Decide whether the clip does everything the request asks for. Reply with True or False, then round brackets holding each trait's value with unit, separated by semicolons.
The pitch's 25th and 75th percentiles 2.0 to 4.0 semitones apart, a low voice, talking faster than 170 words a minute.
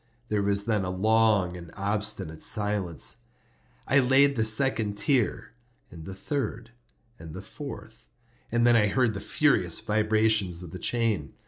False (3.1 semitones; 105 Hz; 150 wpm)